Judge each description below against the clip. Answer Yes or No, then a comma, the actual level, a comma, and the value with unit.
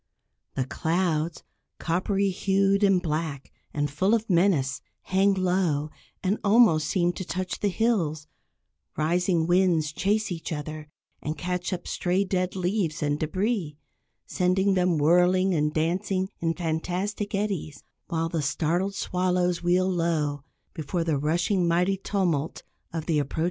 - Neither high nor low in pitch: Yes, medium, 175 Hz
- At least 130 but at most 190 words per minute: Yes, average, 140 wpm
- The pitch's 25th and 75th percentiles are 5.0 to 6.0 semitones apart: No, average, 3.3 semitones